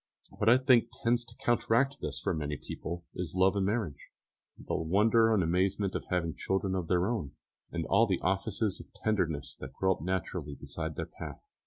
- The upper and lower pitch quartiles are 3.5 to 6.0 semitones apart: Yes, average, 5.1 semitones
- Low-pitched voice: Yes, very low, 95 Hz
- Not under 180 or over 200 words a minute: Yes, average, 190 wpm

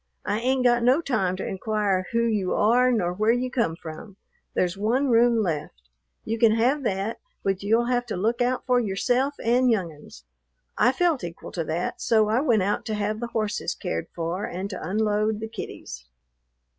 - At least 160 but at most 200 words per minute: Yes, average, 195 wpm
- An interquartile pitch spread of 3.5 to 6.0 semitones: Yes, average, 4.2 semitones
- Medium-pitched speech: No, high, 215 Hz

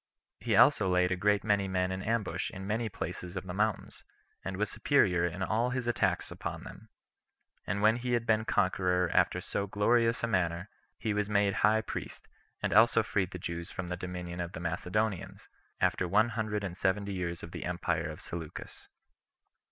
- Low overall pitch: Yes, very low, 95 Hz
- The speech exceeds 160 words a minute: Yes, average, 190 wpm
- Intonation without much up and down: No, average, 3.3 semitones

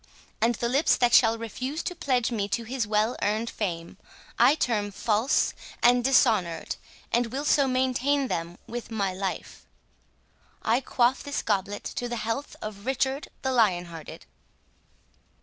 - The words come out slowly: No, average, 150 wpm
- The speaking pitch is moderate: No, high, 235 Hz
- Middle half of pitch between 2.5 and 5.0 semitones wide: Yes, average, 3.8 semitones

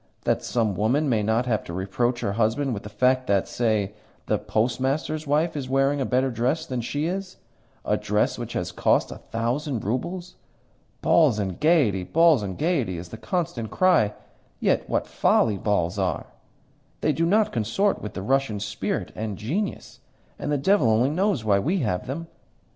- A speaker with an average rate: Yes, average, 180 wpm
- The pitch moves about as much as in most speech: No, wide, 6.4 semitones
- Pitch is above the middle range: No, low, 125 Hz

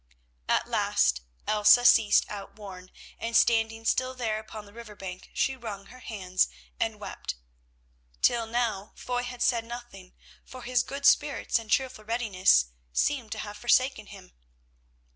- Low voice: No, high, 225 Hz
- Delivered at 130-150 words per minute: Yes, average, 145 wpm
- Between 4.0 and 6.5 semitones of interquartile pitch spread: No, average, 3.3 semitones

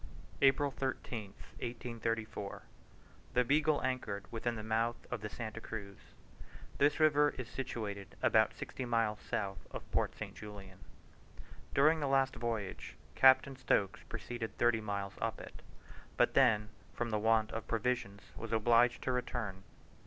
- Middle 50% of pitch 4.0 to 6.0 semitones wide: No, average, 3.2 semitones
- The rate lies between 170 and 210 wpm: No, average, 140 wpm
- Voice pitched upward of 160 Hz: No, low, 115 Hz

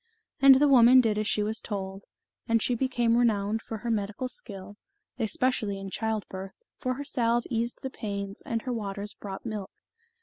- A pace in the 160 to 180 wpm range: Yes, average, 175 wpm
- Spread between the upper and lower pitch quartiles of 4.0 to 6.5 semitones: No, average, 3.1 semitones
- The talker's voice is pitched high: Yes, high, 220 Hz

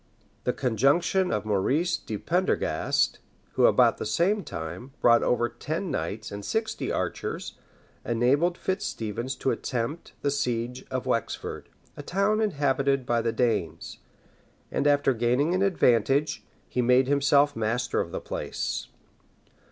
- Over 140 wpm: No, slow, 135 wpm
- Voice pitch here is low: Yes, low, 130 Hz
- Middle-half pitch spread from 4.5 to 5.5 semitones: Yes, average, 4.9 semitones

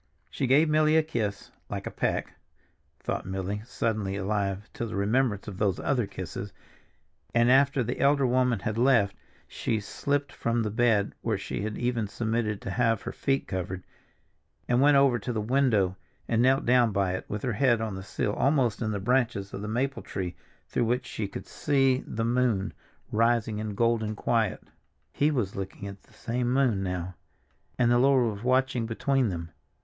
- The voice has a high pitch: No, low, 115 Hz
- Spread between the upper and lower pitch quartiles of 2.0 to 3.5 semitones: No, average, 4.0 semitones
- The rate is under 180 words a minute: No, average, 185 wpm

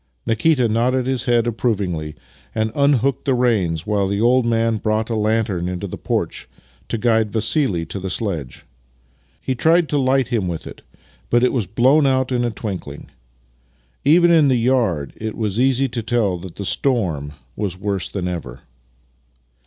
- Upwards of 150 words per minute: Yes, average, 170 wpm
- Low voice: Yes, low, 115 Hz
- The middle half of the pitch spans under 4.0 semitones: No, average, 4.9 semitones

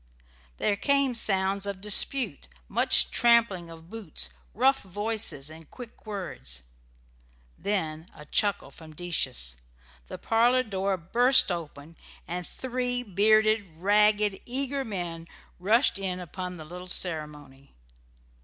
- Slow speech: Yes, slow, 115 wpm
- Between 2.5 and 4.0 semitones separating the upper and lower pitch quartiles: No, average, 5.3 semitones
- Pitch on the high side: Yes, high, 195 Hz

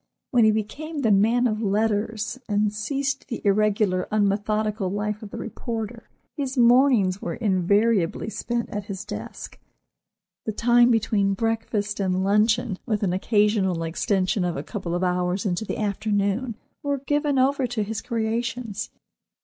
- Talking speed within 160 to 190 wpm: No, average, 150 wpm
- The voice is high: Yes, high, 215 Hz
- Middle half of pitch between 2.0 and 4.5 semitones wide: Yes, average, 2.8 semitones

